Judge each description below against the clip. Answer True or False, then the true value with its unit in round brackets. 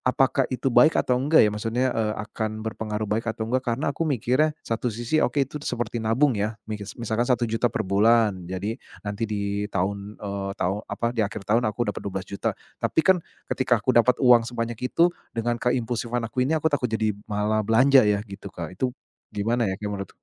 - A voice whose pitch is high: False (115 Hz)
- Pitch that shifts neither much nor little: True (3.2 semitones)